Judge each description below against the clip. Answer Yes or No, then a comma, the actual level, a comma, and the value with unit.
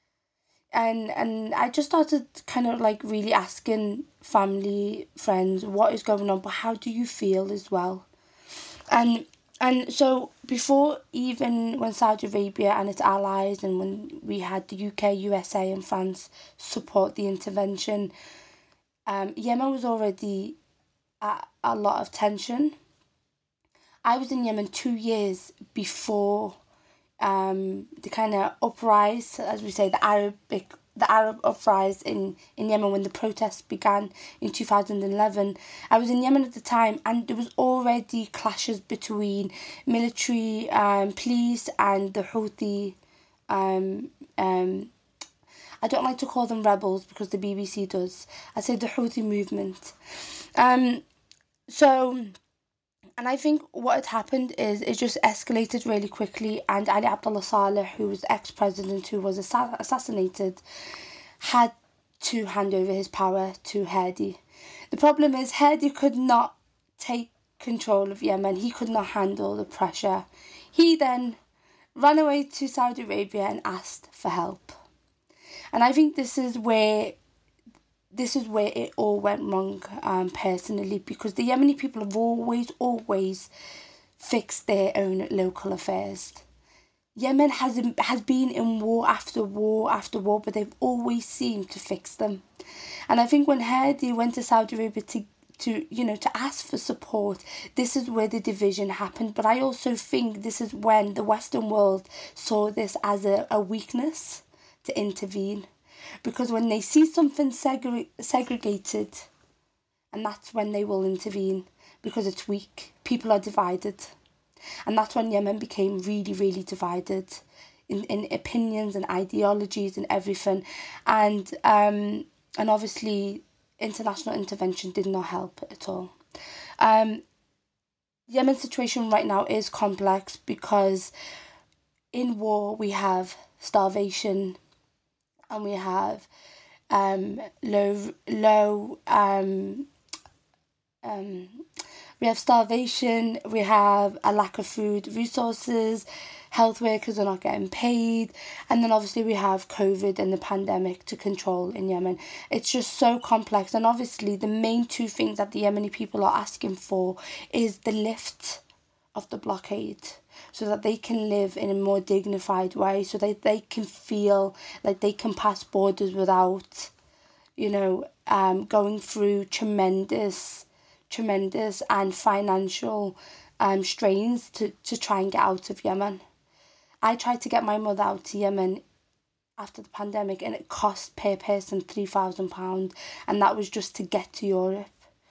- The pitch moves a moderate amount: Yes, average, 3.4 semitones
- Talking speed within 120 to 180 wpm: Yes, average, 150 wpm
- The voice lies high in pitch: Yes, high, 210 Hz